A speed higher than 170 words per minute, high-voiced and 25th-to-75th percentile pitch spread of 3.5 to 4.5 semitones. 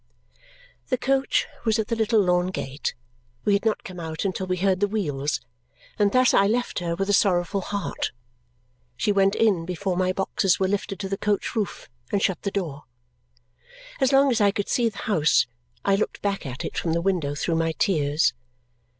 No: average, 195 wpm; high, 195 Hz; average, 3.1 semitones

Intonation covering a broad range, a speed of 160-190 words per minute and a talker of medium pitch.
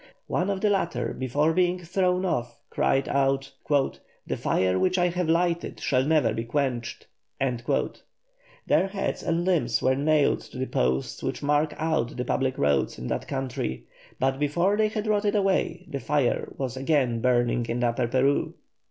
Yes: wide, 6.3 semitones; average, 165 wpm; medium, 145 Hz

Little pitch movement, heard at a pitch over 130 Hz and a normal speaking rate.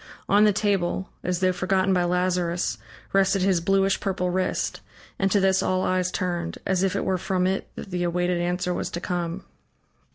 Yes: narrow, 1.4 semitones; medium, 185 Hz; average, 190 wpm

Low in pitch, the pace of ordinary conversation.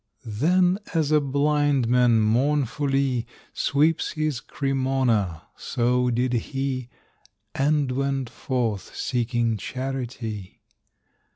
No: low, 130 Hz; slow, 90 wpm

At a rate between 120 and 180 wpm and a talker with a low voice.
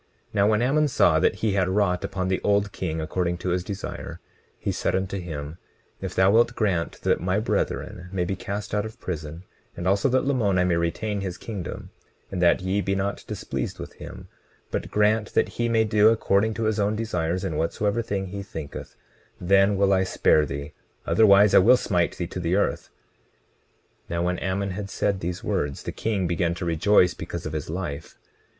No: average, 200 wpm; very low, 95 Hz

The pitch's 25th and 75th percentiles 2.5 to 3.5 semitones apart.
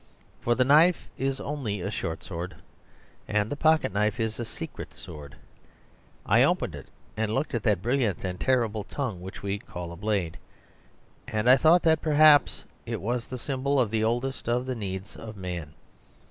No: average, 5.2 semitones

